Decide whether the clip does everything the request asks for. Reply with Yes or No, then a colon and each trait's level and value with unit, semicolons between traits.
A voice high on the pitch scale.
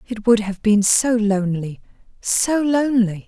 Yes: high, 220 Hz